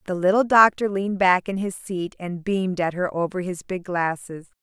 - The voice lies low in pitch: No, medium, 185 Hz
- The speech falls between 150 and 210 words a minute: Yes, fast, 205 wpm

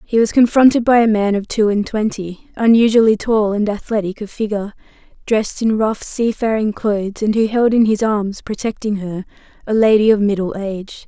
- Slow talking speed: No, average, 185 wpm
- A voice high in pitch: Yes, high, 215 Hz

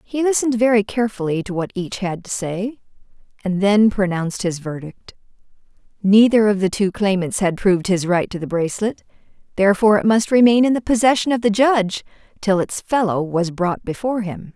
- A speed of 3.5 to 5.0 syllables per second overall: No, 5.6 syllables/s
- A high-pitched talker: Yes, high, 205 Hz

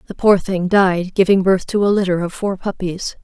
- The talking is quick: Yes, fast, 225 wpm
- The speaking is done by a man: No, female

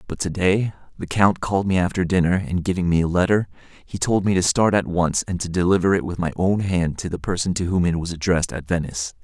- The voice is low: Yes, very low, 90 Hz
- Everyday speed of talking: No, fast, 255 wpm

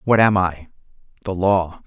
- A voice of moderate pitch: No, very low, 95 Hz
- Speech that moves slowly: Yes, slow, 130 wpm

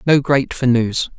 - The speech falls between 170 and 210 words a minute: Yes, fast, 205 wpm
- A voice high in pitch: No, low, 130 Hz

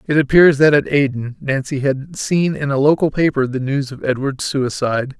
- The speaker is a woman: No, male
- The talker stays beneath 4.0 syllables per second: No, 5.0 syllables/s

